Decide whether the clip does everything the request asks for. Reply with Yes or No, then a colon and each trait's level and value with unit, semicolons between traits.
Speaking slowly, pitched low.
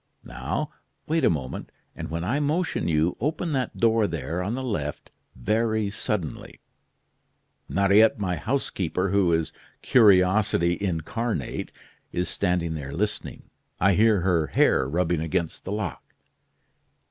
Yes: slow, 130 wpm; very low, 95 Hz